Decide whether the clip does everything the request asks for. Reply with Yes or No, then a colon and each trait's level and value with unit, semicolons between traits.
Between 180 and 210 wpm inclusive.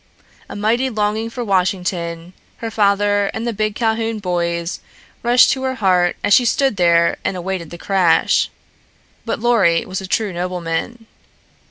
No: average, 155 wpm